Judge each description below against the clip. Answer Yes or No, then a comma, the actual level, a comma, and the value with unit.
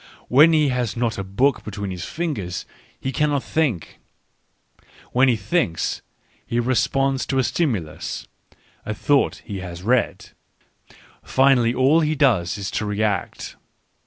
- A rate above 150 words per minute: No, average, 140 wpm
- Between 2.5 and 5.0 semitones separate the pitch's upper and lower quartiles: No, wide, 5.4 semitones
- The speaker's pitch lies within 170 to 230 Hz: No, low, 120 Hz